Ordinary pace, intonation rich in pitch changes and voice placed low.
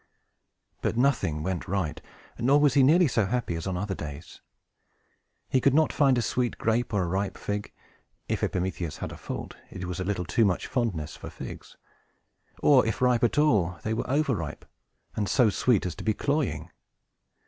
Yes: average, 190 wpm; wide, 6.0 semitones; low, 110 Hz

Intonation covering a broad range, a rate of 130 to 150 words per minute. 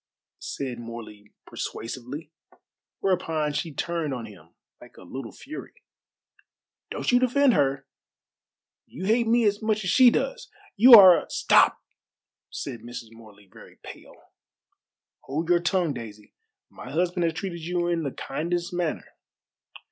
Yes: wide, 7.5 semitones; average, 140 wpm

